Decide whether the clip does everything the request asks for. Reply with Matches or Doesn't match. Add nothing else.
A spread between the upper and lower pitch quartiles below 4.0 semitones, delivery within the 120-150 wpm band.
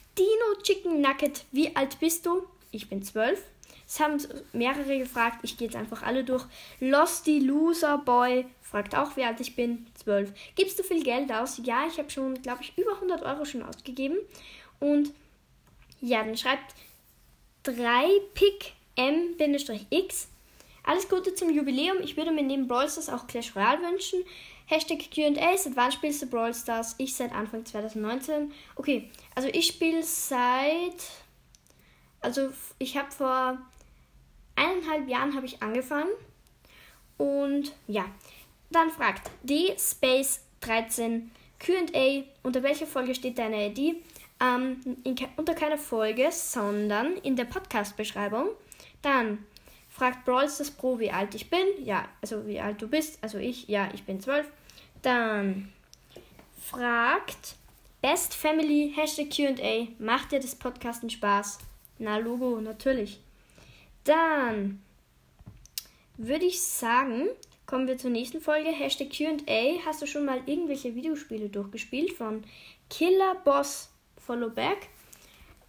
Doesn't match